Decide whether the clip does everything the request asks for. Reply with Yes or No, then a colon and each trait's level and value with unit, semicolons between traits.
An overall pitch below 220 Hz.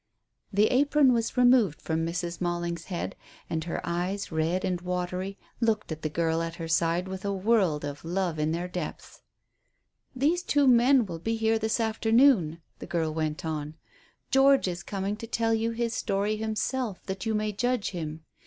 Yes: high, 190 Hz